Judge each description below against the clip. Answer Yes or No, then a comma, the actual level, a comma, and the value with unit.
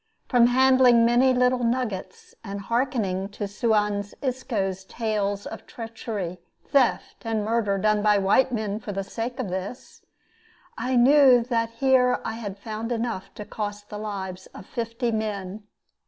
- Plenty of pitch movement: No, average, 3.3 semitones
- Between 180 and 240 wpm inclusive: No, average, 150 wpm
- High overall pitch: Yes, high, 220 Hz